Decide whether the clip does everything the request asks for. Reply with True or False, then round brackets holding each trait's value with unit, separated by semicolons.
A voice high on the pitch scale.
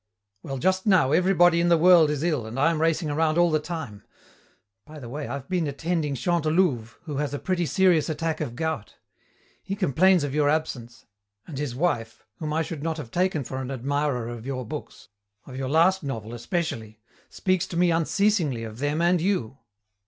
False (155 Hz)